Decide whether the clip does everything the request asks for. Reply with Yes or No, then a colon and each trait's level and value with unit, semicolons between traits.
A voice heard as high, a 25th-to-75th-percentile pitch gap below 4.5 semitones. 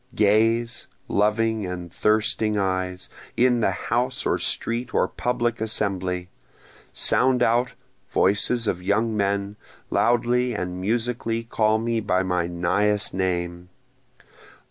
No: low, 105 Hz; average, 3.9 semitones